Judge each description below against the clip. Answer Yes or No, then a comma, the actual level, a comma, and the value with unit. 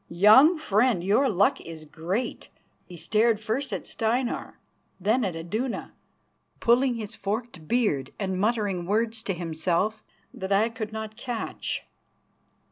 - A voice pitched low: No, high, 215 Hz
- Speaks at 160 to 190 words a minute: No, slow, 135 wpm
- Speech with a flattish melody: No, average, 4.1 semitones